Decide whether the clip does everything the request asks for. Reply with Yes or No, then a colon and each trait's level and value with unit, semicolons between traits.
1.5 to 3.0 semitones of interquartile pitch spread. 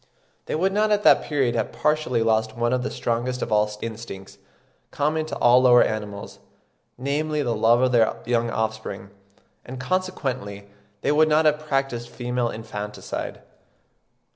No: average, 4.8 semitones